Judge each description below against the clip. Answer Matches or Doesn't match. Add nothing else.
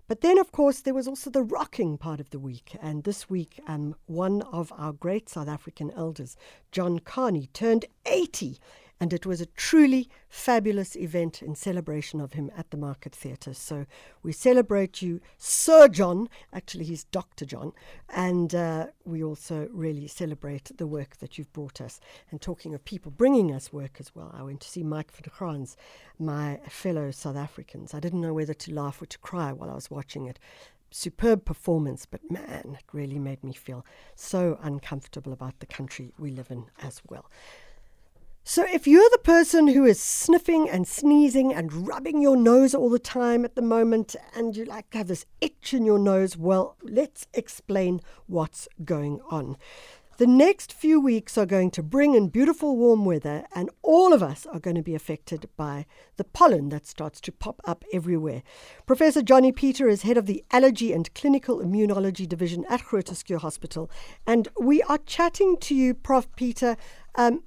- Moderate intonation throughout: Doesn't match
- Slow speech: Doesn't match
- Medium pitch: Matches